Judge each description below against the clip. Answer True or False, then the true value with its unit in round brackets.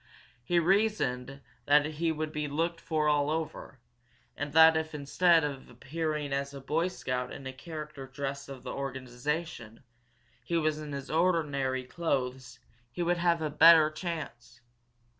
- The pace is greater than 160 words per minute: False (145 wpm)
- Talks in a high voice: False (150 Hz)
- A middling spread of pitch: True (3.1 semitones)